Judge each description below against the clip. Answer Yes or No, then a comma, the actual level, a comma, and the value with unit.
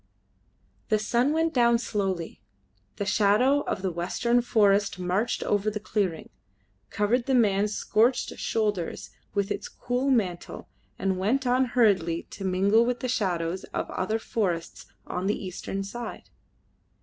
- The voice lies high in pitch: Yes, high, 210 Hz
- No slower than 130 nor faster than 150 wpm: Yes, average, 140 wpm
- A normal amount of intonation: Yes, average, 4.0 semitones